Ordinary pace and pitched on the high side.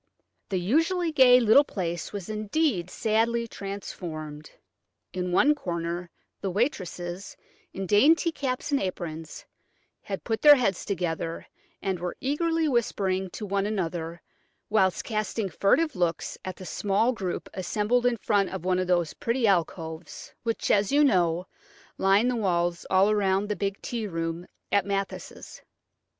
Yes: average, 145 wpm; high, 195 Hz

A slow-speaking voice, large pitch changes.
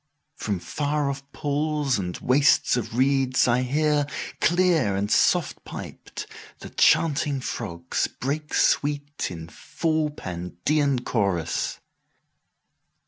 Yes: slow, 95 wpm; wide, 6.3 semitones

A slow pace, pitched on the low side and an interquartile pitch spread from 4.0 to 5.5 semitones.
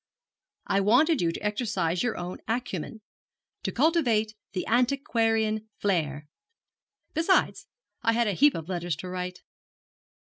No: slow, 130 wpm; high, 215 Hz; average, 5.1 semitones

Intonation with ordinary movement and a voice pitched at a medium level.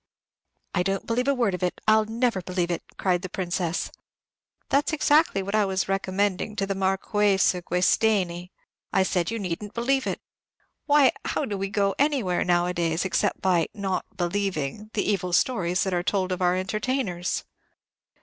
No: average, 3.0 semitones; high, 195 Hz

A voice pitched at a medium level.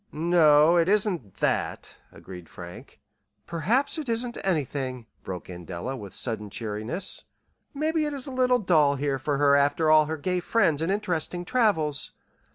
Yes: medium, 155 Hz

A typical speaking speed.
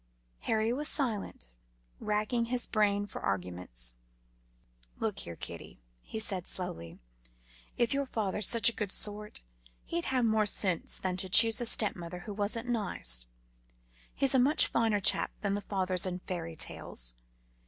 Yes: average, 150 wpm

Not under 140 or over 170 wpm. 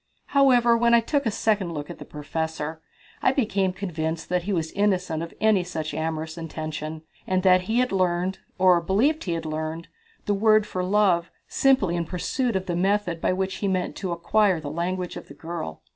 No: average, 200 wpm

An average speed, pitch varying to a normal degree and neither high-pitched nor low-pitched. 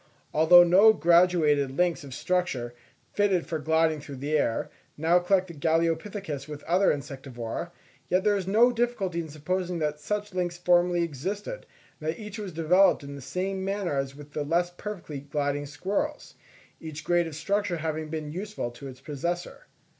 Yes: average, 175 wpm; average, 4.1 semitones; medium, 170 Hz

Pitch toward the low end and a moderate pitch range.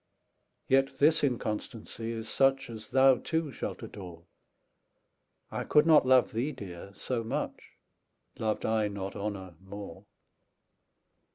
Yes: low, 115 Hz; average, 4.9 semitones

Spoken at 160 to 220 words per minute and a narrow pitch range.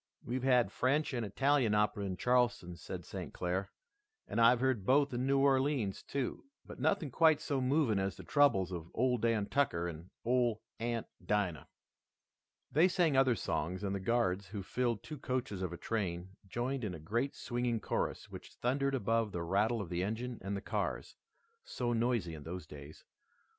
No: average, 180 wpm; average, 5.1 semitones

